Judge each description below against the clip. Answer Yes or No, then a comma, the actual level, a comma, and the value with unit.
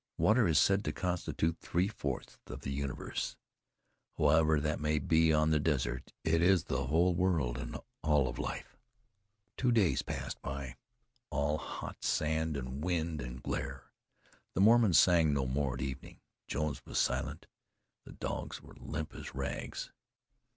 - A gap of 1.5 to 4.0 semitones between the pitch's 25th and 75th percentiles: Yes, average, 3.6 semitones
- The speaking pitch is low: Yes, very low, 75 Hz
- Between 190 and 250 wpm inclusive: No, average, 155 wpm